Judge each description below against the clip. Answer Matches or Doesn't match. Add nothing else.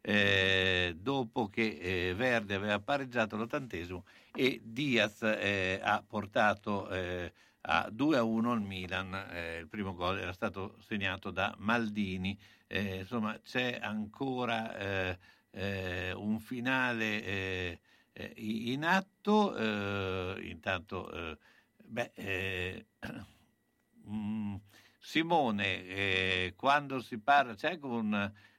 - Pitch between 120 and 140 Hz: Doesn't match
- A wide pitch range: Doesn't match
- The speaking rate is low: Matches